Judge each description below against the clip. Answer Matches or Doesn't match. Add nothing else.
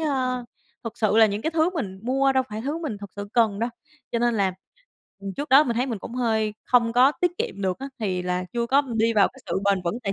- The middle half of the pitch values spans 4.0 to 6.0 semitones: Matches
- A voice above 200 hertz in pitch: Matches